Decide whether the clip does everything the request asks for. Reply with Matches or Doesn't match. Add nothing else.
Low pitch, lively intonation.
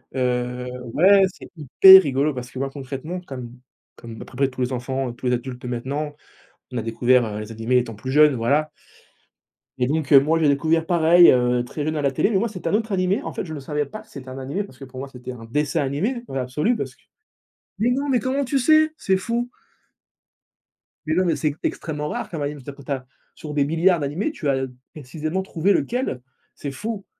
Doesn't match